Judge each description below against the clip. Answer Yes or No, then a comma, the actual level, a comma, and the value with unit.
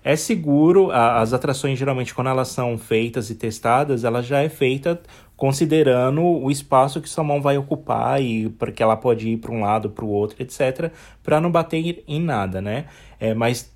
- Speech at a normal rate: No, fast, 190 wpm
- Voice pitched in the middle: No, low, 130 Hz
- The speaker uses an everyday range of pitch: Yes, average, 4.4 semitones